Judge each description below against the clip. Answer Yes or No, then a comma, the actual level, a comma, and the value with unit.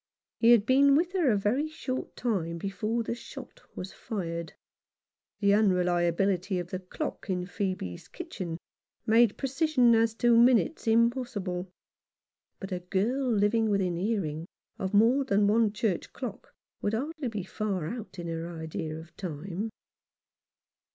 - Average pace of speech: Yes, average, 145 wpm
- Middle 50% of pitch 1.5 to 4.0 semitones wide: No, average, 4.8 semitones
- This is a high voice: Yes, high, 205 Hz